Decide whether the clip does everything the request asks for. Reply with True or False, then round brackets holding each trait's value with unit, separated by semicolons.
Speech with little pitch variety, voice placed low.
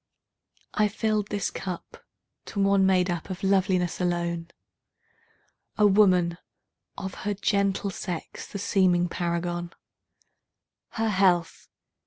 False (2.3 semitones; 190 Hz)